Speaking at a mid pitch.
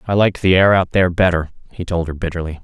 No: very low, 90 Hz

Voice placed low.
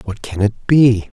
Yes: low, 110 Hz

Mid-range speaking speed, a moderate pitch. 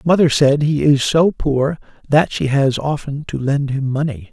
Yes: average, 195 wpm; medium, 145 Hz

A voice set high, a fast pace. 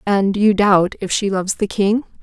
Yes: high, 200 Hz; fast, 215 wpm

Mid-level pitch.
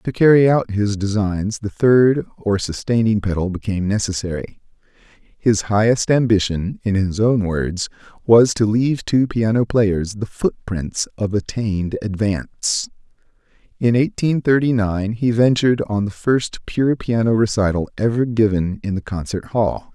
No: low, 110 Hz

